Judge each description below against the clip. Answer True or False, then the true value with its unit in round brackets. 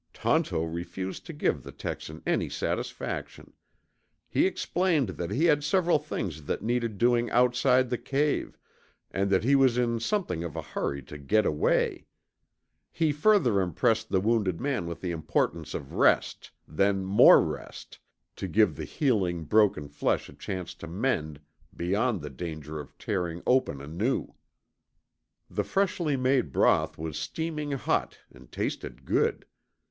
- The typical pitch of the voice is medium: False (100 Hz)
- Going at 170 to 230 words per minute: False (150 wpm)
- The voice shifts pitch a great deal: True (8.0 semitones)